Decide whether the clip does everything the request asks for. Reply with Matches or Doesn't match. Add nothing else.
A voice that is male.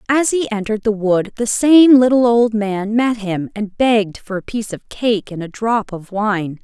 Doesn't match